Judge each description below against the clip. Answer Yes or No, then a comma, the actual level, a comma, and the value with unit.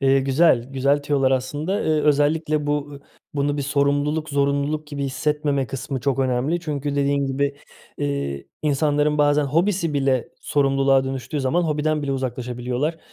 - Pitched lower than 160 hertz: Yes, medium, 140 Hz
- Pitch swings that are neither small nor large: No, narrow, 1.8 semitones